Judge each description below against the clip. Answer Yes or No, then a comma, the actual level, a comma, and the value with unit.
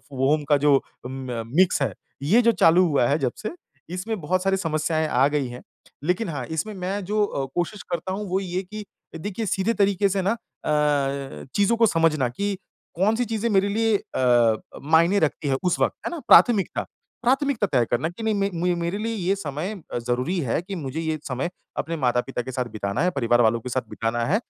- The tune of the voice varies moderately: No, wide, 7.0 semitones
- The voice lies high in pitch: No, medium, 165 Hz